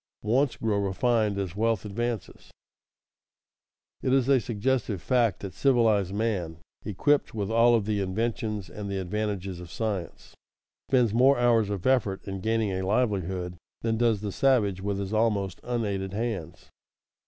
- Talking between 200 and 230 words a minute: No, average, 155 wpm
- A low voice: Yes, low, 105 Hz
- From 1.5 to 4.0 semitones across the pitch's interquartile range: Yes, average, 3.3 semitones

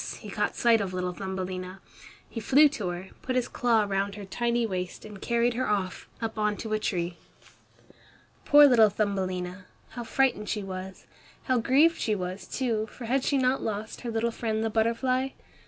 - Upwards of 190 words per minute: No, average, 185 wpm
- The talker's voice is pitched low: No, high, 215 Hz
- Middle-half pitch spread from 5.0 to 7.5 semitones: No, average, 3.9 semitones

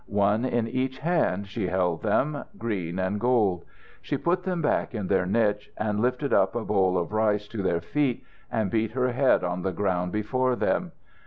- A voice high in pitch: No, low, 105 Hz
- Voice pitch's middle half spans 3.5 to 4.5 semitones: No, average, 5.0 semitones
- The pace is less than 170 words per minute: No, average, 190 wpm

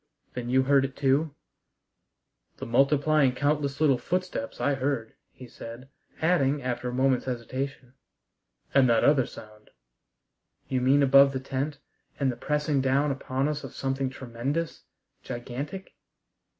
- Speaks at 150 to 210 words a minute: No, average, 140 wpm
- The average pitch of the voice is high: No, low, 135 Hz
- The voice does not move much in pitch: Yes, narrow, 2.1 semitones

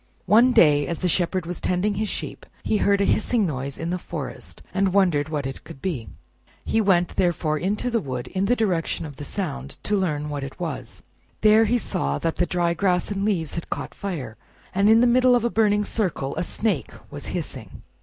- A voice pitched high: No, medium, 180 Hz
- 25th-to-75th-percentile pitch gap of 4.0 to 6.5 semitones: Yes, wide, 5.5 semitones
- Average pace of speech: No, fast, 215 wpm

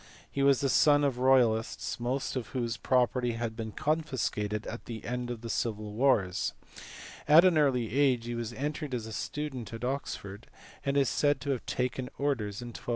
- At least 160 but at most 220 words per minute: Yes, average, 195 wpm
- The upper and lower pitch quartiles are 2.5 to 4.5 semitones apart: Yes, average, 3.3 semitones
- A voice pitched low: Yes, low, 125 Hz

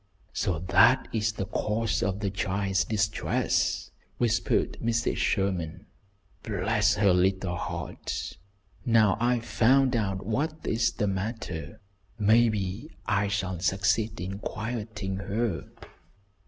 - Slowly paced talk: Yes, slow, 115 wpm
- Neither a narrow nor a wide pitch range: Yes, average, 3.0 semitones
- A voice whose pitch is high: No, low, 105 Hz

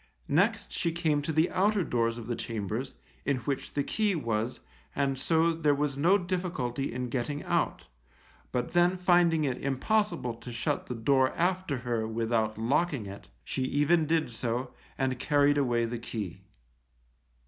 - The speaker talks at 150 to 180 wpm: Yes, average, 160 wpm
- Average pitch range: No, wide, 5.9 semitones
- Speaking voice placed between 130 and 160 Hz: Yes, medium, 140 Hz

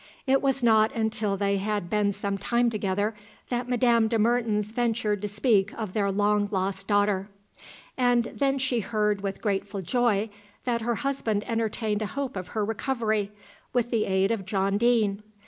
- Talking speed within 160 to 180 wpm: Yes, average, 170 wpm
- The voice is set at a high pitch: Yes, high, 215 Hz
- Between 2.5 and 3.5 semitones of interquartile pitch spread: Yes, average, 2.8 semitones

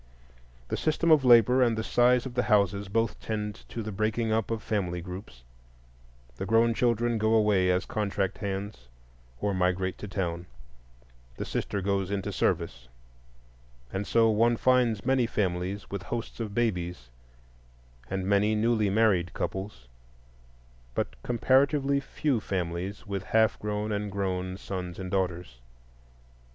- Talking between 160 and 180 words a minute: No, average, 140 wpm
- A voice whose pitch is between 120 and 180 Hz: No, low, 105 Hz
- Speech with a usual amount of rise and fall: Yes, average, 3.5 semitones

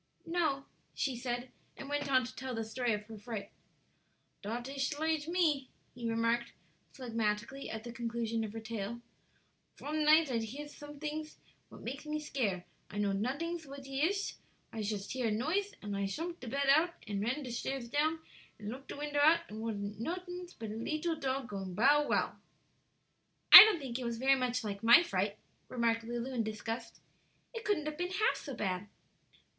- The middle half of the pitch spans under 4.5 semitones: No, average, 4.9 semitones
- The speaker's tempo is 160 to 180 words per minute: No, average, 190 wpm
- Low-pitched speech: No, very high, 255 Hz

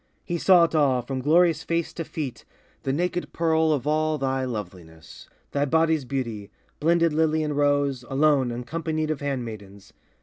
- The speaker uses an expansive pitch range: No, average, 3.8 semitones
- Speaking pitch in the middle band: Yes, medium, 145 Hz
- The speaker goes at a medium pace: Yes, average, 160 wpm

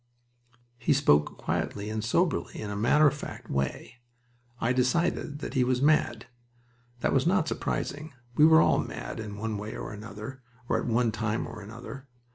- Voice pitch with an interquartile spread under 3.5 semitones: No, average, 5.2 semitones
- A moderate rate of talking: Yes, average, 175 wpm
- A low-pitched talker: Yes, low, 120 Hz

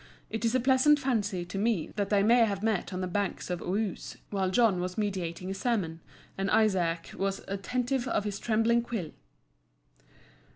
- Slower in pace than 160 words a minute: No, average, 175 wpm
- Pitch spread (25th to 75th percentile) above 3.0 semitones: Yes, average, 3.8 semitones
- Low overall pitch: No, high, 205 Hz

